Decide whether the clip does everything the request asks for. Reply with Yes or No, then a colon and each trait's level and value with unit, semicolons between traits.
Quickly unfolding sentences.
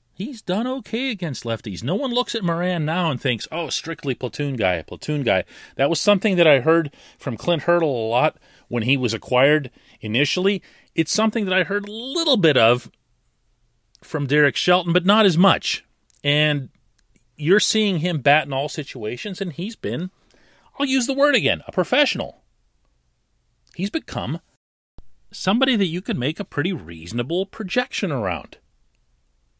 No: average, 165 wpm